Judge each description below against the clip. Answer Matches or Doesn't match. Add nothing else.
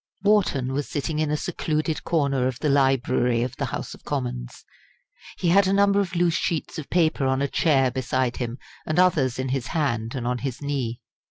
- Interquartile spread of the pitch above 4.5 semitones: Doesn't match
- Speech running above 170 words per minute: Matches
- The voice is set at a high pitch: Doesn't match